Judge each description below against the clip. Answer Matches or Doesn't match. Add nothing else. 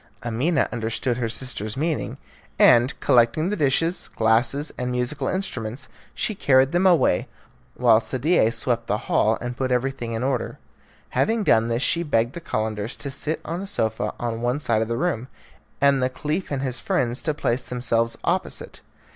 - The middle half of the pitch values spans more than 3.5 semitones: Matches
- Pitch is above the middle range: Doesn't match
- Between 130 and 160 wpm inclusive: Doesn't match